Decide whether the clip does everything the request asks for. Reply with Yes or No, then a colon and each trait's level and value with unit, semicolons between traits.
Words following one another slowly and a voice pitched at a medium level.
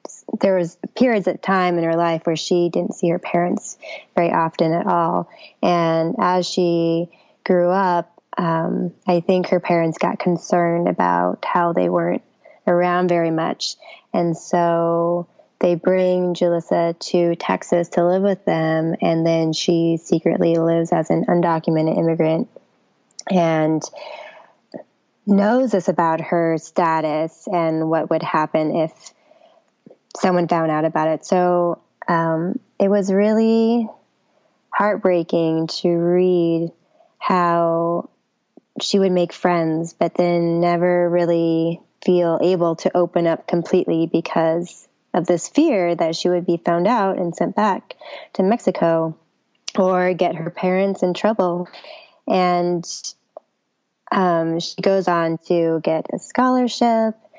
Yes: slow, 130 wpm; medium, 175 Hz